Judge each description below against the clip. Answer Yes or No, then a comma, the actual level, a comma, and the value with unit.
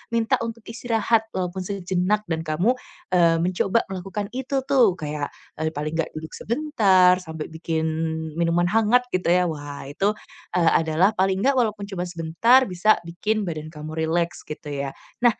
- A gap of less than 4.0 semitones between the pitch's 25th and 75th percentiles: No, average, 4.9 semitones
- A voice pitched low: No, medium, 180 Hz